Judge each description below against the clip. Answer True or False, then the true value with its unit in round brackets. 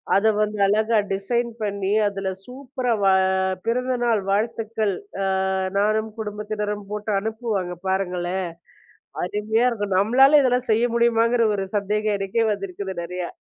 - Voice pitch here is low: False (210 Hz)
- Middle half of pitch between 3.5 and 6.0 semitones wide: False (2.8 semitones)